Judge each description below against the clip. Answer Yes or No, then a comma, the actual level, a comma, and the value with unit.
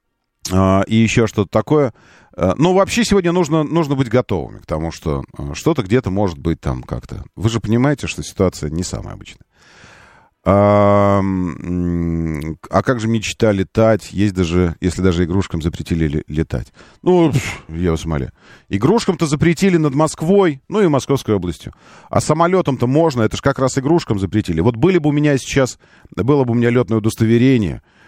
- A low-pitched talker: Yes, low, 110 Hz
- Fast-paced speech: Yes, fast, 165 wpm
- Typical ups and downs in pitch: No, wide, 7.8 semitones